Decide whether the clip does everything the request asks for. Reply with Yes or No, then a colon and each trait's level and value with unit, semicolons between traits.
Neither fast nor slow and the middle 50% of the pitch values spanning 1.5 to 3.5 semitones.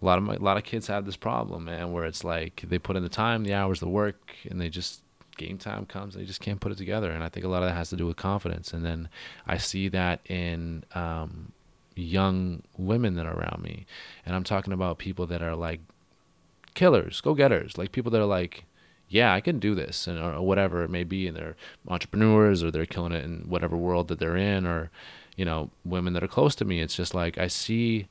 No: fast, 250 wpm; narrow, 2.5 semitones